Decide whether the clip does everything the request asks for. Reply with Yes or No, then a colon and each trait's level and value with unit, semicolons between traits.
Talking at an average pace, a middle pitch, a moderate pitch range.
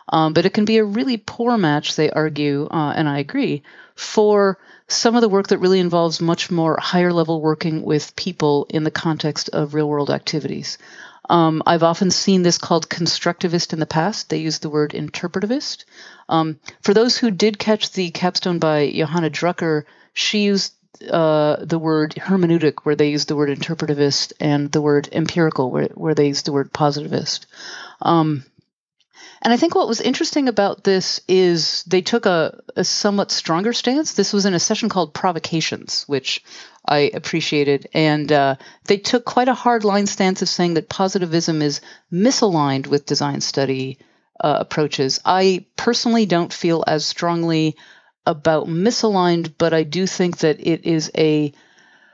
Yes: average, 170 wpm; medium, 170 Hz; average, 4.4 semitones